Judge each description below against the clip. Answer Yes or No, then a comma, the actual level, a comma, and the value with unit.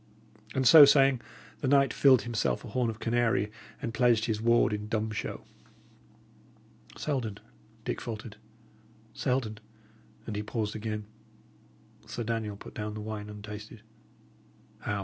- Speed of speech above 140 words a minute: No, slow, 135 wpm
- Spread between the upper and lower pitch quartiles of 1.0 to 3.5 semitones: Yes, narrow, 2.5 semitones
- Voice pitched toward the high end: No, low, 110 Hz